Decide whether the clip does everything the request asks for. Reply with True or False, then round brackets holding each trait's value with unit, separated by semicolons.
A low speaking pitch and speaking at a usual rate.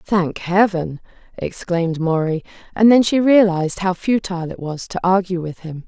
False (180 Hz; 165 wpm)